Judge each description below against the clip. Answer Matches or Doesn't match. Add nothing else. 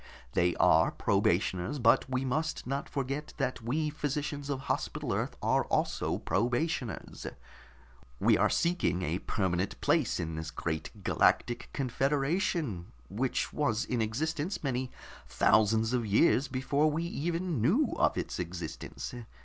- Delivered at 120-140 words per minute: Matches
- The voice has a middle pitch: Doesn't match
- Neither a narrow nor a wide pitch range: Doesn't match